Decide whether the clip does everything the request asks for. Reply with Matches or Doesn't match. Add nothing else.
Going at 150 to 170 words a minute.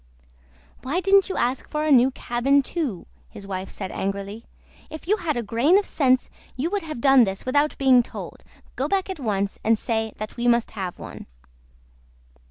Doesn't match